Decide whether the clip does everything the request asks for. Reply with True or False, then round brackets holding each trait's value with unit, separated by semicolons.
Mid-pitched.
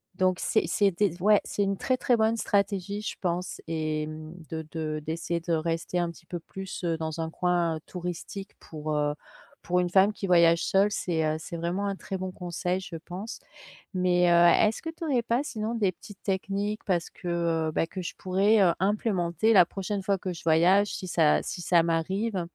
True (180 Hz)